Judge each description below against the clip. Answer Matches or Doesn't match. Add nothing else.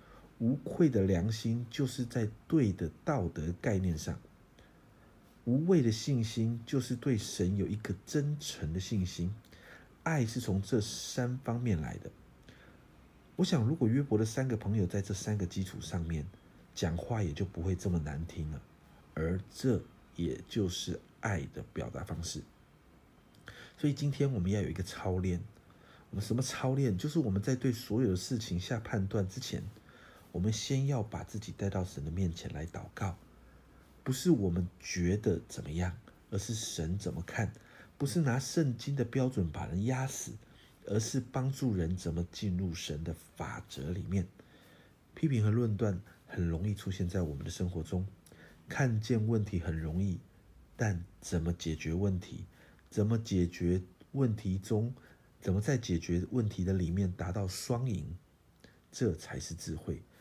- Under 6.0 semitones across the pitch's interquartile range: Matches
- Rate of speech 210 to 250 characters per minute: Matches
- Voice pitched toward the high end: Doesn't match